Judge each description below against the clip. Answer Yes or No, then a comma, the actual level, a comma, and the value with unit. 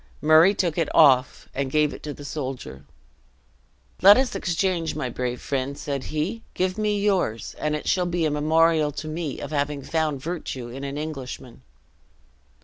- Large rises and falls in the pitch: No, average, 3.7 semitones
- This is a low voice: No, medium, 150 Hz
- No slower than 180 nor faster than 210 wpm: No, average, 170 wpm